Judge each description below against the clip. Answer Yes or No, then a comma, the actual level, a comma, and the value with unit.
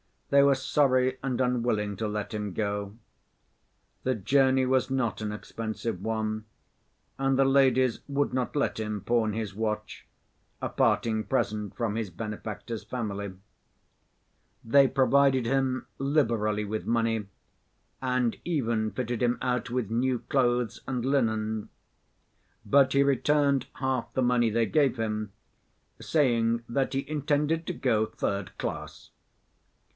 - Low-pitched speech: Yes, low, 120 Hz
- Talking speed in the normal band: No, slow, 130 wpm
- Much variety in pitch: No, average, 3.5 semitones